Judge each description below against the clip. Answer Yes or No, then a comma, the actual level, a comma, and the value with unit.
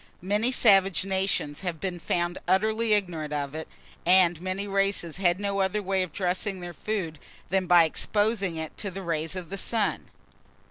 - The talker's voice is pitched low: No, medium, 185 Hz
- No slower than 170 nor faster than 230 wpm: Yes, average, 175 wpm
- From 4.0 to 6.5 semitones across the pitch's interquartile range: No, narrow, 2.4 semitones